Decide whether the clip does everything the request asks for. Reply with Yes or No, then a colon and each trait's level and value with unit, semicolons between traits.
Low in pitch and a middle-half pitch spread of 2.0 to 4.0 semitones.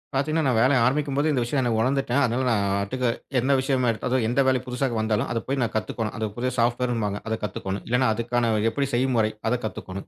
Yes: low, 120 Hz; average, 2.9 semitones